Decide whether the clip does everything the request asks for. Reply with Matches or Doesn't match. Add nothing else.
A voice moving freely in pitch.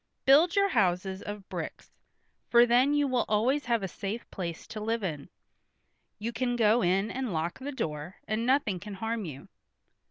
Doesn't match